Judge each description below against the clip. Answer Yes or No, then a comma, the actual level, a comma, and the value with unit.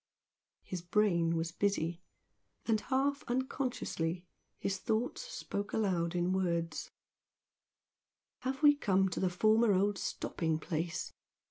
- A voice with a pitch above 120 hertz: Yes, high, 190 Hz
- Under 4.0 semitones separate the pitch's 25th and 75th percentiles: No, average, 4.7 semitones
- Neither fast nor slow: No, slow, 115 wpm